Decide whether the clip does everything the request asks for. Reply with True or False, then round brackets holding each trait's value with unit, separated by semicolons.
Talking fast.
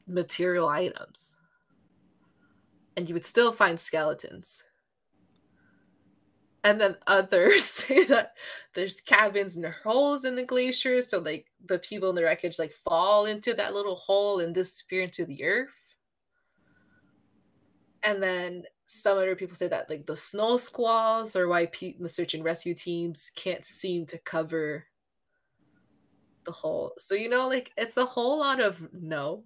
False (150 wpm)